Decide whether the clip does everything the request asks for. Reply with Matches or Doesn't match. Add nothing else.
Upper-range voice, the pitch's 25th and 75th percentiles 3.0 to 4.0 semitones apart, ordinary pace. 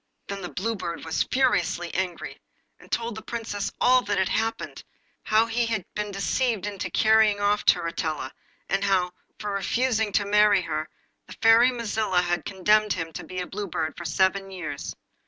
Matches